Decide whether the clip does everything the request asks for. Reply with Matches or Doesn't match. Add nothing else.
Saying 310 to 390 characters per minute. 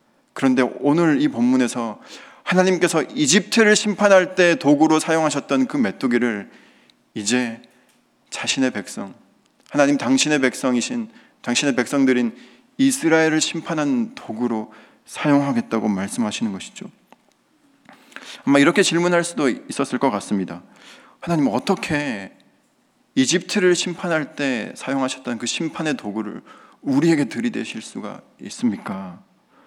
Doesn't match